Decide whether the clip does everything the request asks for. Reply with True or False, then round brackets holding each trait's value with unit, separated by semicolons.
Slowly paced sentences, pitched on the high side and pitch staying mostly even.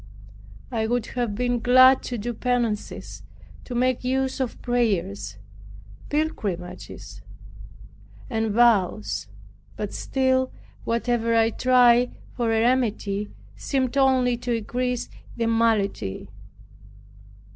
True (105 wpm; 240 Hz; 2.3 semitones)